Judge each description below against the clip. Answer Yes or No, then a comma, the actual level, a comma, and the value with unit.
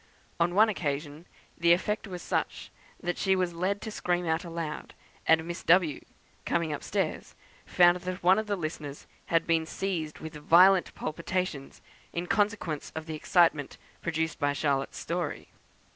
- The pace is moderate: Yes, average, 160 wpm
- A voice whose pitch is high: No, medium, 170 Hz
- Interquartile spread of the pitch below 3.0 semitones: Yes, narrow, 2.6 semitones